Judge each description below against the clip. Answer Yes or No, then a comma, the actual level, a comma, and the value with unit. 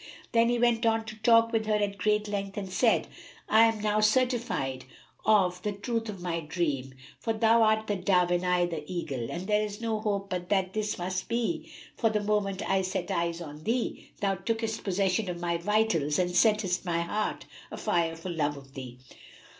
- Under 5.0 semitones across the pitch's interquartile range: Yes, average, 3.7 semitones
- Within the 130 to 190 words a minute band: No, average, 200 wpm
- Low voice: No, high, 200 Hz